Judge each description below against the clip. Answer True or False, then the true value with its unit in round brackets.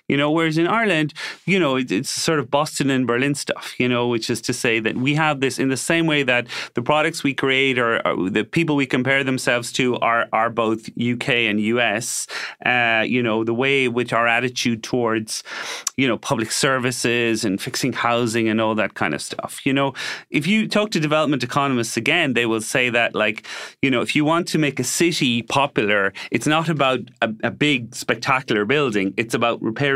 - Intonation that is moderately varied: True (3.7 semitones)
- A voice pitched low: True (130 Hz)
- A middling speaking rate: False (210 wpm)